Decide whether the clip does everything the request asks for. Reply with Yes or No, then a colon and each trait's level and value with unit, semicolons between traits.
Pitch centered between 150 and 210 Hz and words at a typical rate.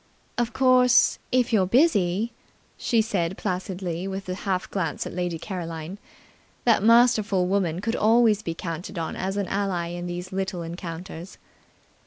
Yes: high, 190 Hz; average, 155 wpm